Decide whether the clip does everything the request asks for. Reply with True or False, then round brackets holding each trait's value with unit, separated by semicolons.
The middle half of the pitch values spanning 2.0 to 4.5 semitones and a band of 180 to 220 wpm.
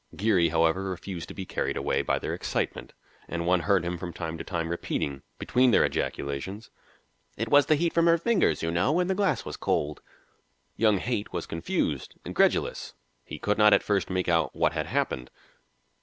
False (5.2 semitones; 190 wpm)